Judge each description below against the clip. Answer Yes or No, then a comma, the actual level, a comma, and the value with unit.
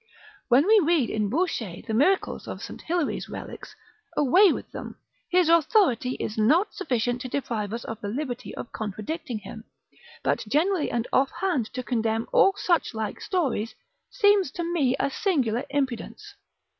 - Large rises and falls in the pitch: Yes, wide, 7.2 semitones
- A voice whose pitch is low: No, very high, 270 Hz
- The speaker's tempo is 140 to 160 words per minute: Yes, average, 155 wpm